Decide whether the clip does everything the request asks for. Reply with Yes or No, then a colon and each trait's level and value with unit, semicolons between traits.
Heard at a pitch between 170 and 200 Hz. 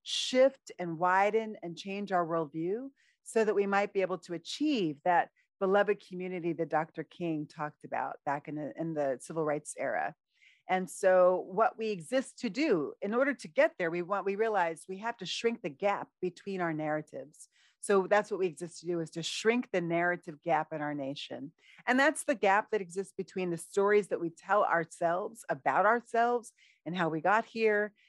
Yes: medium, 185 Hz